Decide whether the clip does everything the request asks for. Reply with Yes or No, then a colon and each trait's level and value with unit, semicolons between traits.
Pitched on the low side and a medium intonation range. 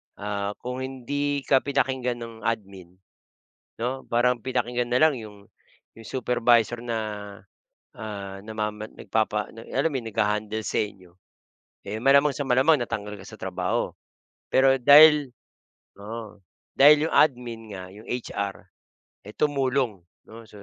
Yes: low, 120 Hz; average, 4.0 semitones